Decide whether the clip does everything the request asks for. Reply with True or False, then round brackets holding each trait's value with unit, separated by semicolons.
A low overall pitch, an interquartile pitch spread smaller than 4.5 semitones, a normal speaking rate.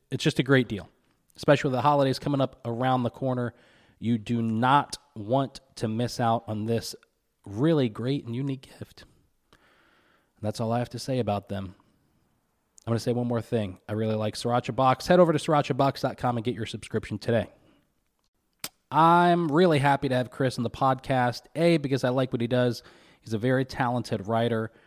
True (125 Hz; 3.1 semitones; 190 wpm)